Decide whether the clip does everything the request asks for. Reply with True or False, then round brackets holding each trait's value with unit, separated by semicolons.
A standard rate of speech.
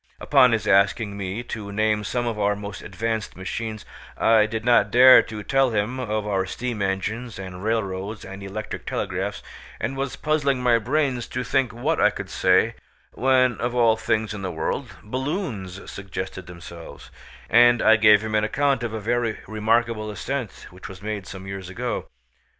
True (175 wpm)